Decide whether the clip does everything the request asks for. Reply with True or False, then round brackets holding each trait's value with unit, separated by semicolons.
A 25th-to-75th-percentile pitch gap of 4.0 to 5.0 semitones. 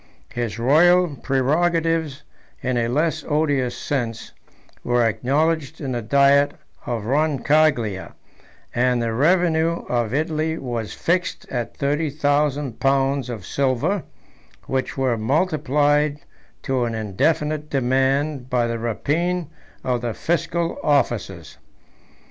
True (4.3 semitones)